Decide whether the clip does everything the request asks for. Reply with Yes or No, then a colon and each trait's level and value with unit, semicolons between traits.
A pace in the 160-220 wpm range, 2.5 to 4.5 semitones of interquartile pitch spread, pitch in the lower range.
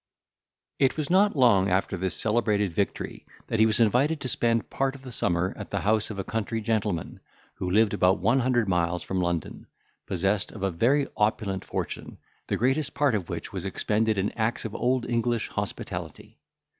Yes: average, 185 wpm; average, 4.2 semitones; low, 110 Hz